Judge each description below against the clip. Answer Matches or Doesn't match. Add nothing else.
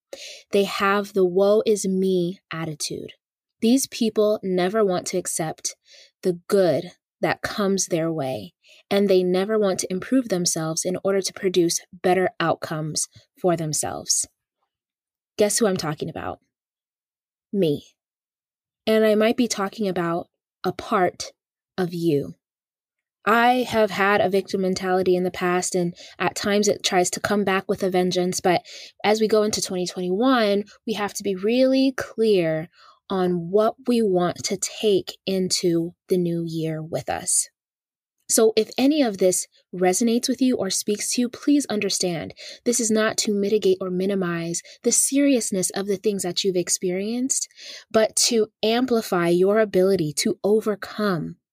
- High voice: Matches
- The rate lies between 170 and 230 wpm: Doesn't match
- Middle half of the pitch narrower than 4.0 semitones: Matches